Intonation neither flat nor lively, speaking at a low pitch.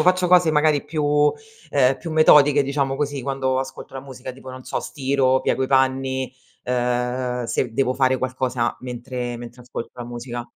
No: narrow, 2.1 semitones; low, 130 Hz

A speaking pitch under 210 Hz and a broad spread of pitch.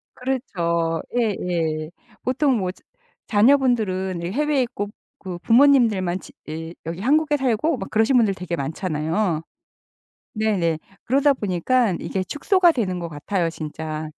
Yes: high, 195 Hz; wide, 7.1 semitones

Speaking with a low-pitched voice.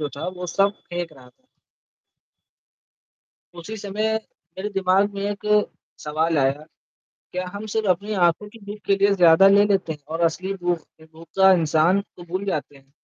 No: medium, 185 Hz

